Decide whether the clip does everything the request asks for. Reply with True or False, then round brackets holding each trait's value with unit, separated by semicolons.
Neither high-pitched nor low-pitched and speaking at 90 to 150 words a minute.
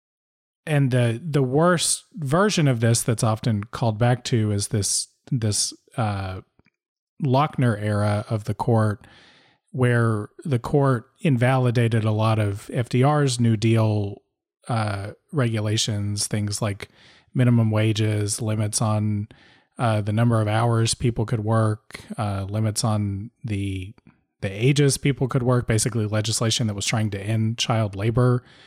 False (115 Hz; 135 wpm)